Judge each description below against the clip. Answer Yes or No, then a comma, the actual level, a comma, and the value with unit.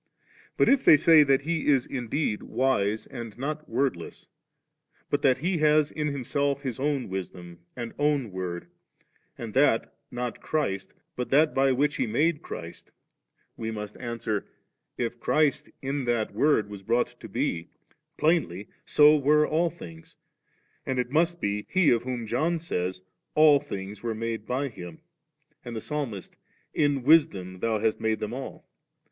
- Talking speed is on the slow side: No, average, 165 wpm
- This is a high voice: No, low, 125 Hz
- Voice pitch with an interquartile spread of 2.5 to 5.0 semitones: No, wide, 5.5 semitones